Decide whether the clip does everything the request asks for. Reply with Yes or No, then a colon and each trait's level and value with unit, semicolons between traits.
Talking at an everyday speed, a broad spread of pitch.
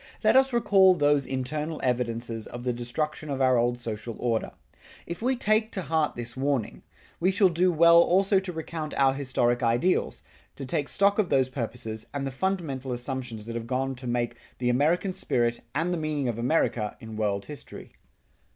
Yes: average, 180 wpm; wide, 5.9 semitones